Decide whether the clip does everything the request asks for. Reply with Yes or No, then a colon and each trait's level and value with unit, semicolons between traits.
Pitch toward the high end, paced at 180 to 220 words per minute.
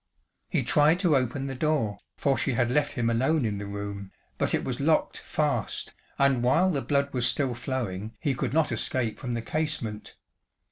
No: low, 130 Hz; average, 190 wpm